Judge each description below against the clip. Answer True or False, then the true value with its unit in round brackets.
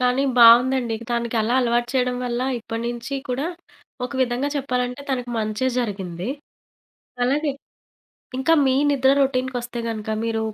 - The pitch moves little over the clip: True (2.0 semitones)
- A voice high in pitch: True (245 Hz)